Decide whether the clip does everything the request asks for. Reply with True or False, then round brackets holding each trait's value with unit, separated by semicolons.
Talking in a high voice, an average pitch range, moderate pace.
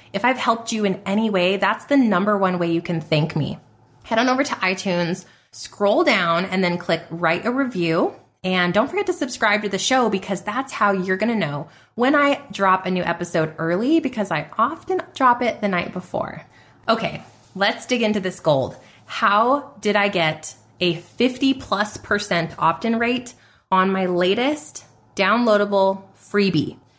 True (195 Hz; 4.9 semitones; 180 wpm)